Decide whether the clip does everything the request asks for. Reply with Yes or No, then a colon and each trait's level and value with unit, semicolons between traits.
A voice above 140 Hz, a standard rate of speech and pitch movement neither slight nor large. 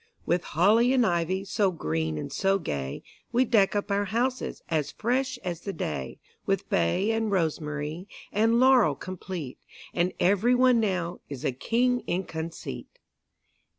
No: high, 190 Hz; average, 150 wpm; wide, 5.9 semitones